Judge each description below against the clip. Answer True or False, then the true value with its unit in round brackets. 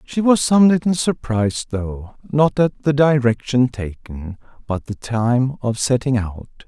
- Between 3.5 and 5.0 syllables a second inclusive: True (4.1 syllables/s)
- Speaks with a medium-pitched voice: False (125 Hz)